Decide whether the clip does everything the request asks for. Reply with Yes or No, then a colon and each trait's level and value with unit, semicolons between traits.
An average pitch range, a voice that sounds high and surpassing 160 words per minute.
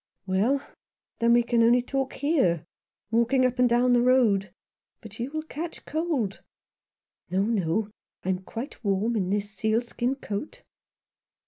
No: average, 4.1 semitones; high, 235 Hz; average, 155 wpm